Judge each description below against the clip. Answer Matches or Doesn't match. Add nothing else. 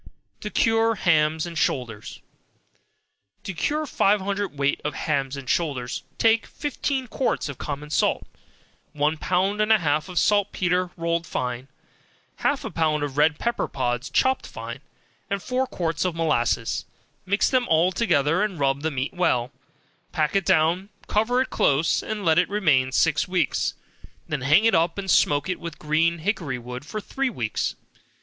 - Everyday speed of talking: Matches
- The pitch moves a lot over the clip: Matches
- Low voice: Doesn't match